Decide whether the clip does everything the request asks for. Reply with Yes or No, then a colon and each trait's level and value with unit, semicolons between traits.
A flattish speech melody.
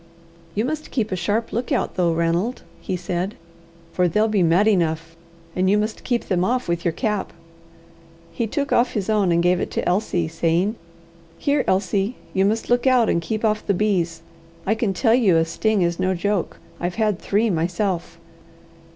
No: average, 4.1 semitones